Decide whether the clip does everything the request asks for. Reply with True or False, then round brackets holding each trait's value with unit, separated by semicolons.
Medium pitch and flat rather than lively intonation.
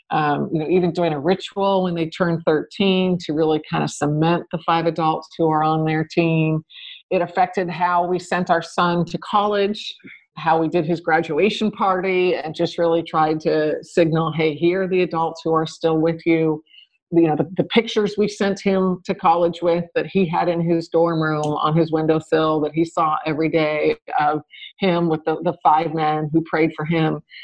True (165 Hz; 2.2 semitones)